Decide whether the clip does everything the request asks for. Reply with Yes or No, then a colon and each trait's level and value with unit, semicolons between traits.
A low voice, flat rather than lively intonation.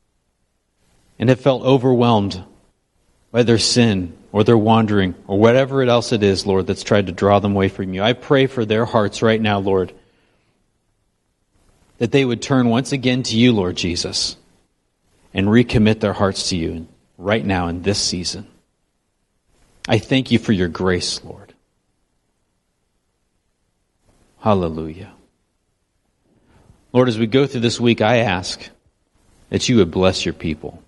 No: low, 100 Hz; average, 4.2 semitones